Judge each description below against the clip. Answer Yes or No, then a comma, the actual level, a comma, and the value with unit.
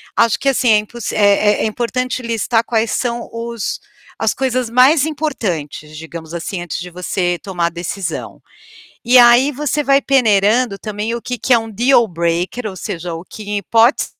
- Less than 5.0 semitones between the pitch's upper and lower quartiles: No, wide, 5.4 semitones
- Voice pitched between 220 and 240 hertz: Yes, high, 225 Hz